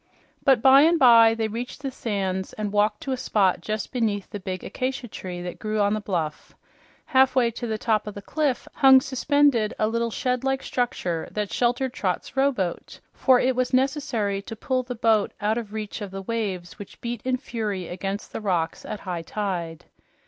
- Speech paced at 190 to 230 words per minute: Yes, average, 195 wpm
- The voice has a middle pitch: No, high, 220 Hz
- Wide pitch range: No, average, 4.2 semitones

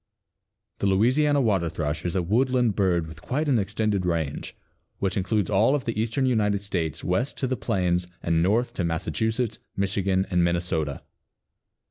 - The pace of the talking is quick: No, average, 165 wpm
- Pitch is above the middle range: No, low, 100 Hz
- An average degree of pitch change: Yes, average, 4.7 semitones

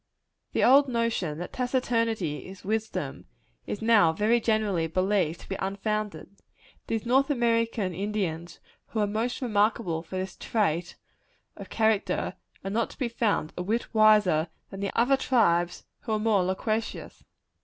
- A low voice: No, high, 210 Hz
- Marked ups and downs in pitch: No, average, 3.6 semitones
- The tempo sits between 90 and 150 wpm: Yes, average, 145 wpm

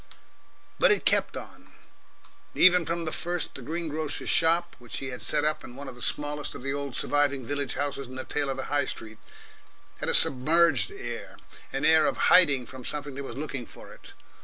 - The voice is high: No, medium, 145 Hz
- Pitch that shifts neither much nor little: Yes, average, 3.2 semitones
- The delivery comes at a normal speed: No, fast, 210 wpm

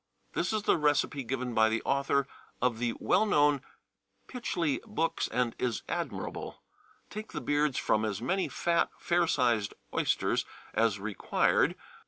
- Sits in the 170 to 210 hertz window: No, low, 135 Hz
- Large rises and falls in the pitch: Yes, wide, 6.3 semitones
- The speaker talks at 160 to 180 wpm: No, average, 150 wpm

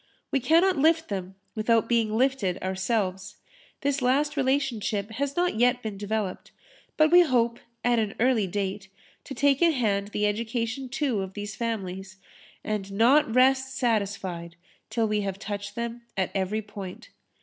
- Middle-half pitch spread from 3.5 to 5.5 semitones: Yes, average, 4.7 semitones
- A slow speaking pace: No, average, 155 wpm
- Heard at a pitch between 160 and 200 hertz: No, high, 225 Hz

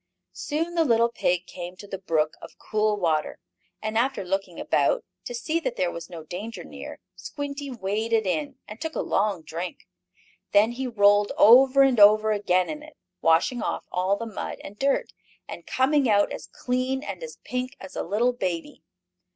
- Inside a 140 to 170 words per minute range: No, average, 185 wpm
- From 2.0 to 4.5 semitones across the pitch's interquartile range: No, wide, 5.6 semitones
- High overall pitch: Yes, high, 215 Hz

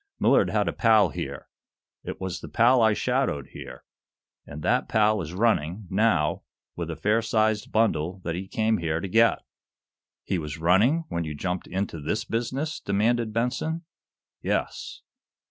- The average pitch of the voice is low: Yes, low, 105 Hz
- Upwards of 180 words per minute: No, average, 160 wpm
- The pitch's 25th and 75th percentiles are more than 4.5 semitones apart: Yes, average, 5.2 semitones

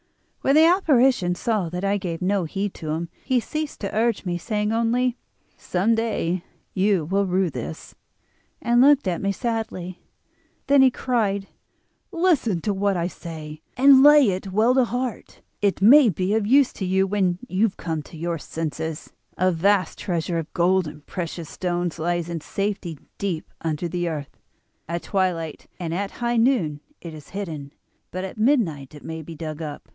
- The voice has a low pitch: No, high, 190 Hz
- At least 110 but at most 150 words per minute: No, average, 175 wpm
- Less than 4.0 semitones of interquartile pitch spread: No, average, 5.2 semitones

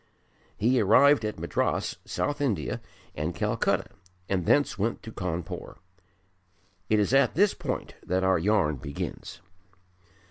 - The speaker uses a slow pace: Yes, slow, 130 wpm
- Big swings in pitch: Yes, wide, 6.1 semitones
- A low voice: Yes, low, 105 Hz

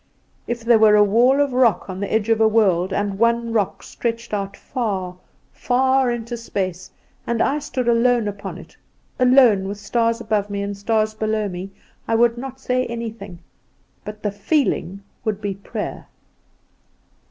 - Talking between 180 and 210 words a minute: No, average, 165 wpm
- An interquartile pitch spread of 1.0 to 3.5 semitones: Yes, average, 2.9 semitones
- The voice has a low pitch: No, high, 220 Hz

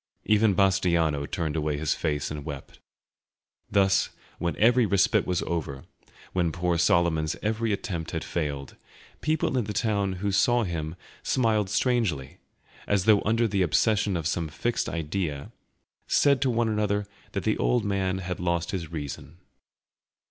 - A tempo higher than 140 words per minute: Yes, average, 150 wpm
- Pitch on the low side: Yes, very low, 95 Hz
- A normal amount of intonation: Yes, average, 4.7 semitones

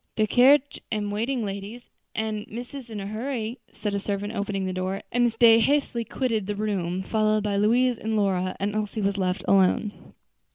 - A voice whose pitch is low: No, high, 215 Hz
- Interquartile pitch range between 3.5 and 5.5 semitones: No, narrow, 2.6 semitones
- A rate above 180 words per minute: Yes, average, 190 wpm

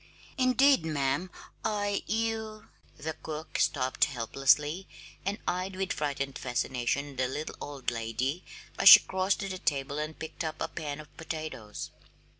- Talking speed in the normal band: Yes, average, 150 wpm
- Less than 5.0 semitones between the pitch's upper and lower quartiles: No, wide, 5.5 semitones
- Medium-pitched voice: Yes, medium, 155 Hz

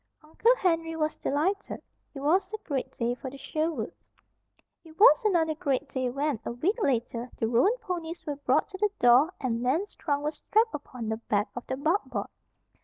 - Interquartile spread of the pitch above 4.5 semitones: Yes, average, 5.3 semitones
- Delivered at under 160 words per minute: No, average, 185 wpm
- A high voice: Yes, very high, 300 Hz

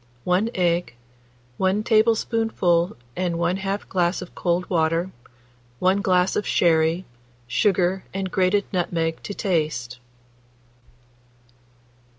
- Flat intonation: Yes, narrow, 2.3 semitones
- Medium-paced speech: No, slow, 100 wpm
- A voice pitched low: No, medium, 180 Hz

